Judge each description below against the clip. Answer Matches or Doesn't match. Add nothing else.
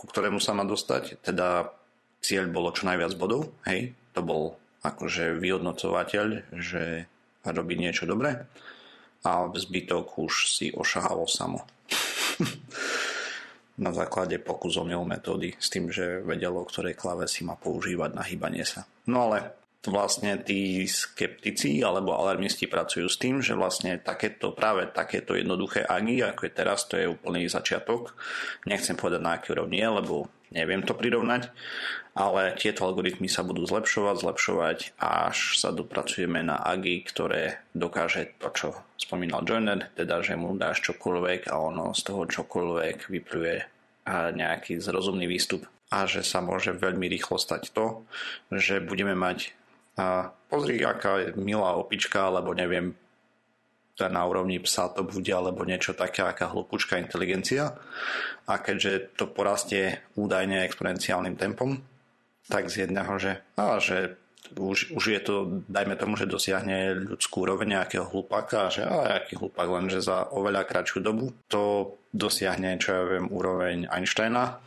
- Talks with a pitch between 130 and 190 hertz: Doesn't match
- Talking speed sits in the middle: Matches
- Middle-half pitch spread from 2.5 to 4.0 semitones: Doesn't match